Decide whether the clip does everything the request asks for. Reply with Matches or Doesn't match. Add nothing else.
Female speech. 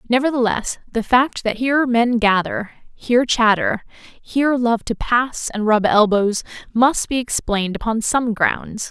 Matches